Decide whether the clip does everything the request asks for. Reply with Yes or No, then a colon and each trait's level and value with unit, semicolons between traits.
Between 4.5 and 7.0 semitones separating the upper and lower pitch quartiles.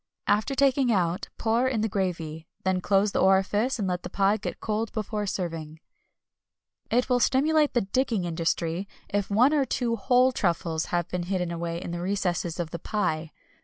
Yes: average, 5.0 semitones